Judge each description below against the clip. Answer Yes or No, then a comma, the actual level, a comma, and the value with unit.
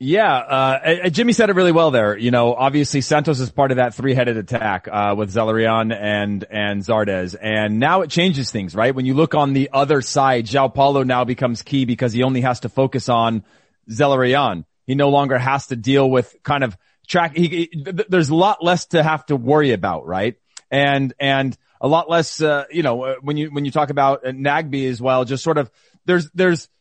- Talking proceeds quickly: Yes, fast, 210 wpm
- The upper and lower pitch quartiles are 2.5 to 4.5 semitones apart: Yes, average, 3.8 semitones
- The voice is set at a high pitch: No, low, 135 Hz